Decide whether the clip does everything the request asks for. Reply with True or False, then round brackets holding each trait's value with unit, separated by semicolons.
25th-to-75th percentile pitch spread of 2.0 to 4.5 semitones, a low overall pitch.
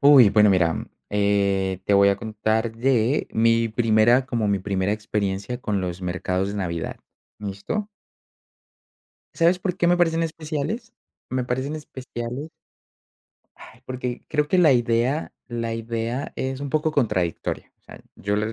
False (5.0 semitones; 115 Hz)